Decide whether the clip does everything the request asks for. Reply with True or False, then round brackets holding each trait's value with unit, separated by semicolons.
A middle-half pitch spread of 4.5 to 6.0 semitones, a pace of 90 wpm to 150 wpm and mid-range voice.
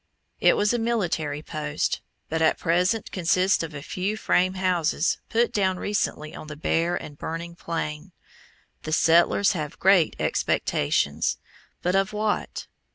False (3.7 semitones; 145 wpm; 175 Hz)